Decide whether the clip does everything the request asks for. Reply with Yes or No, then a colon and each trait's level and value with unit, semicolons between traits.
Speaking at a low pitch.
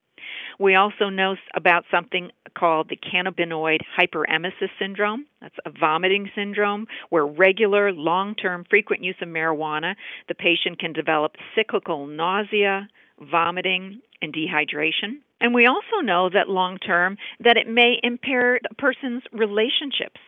No: high, 190 Hz